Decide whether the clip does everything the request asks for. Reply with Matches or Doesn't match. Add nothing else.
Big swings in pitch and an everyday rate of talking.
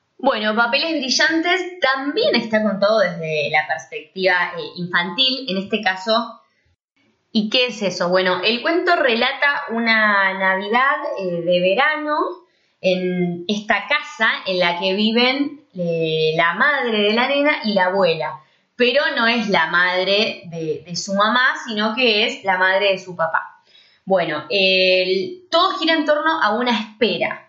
Matches